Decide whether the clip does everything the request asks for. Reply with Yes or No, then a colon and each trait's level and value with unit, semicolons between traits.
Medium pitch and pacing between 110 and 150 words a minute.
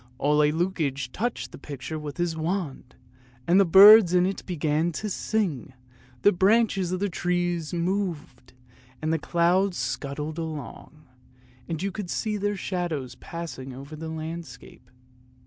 Yes: medium, 170 Hz; average, 140 wpm